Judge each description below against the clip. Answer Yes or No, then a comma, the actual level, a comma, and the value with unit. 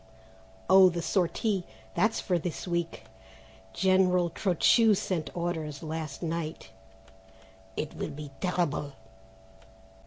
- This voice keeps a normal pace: No, slow, 100 wpm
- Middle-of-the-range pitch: Yes, medium, 170 Hz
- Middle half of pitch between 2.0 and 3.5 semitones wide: Yes, average, 2.9 semitones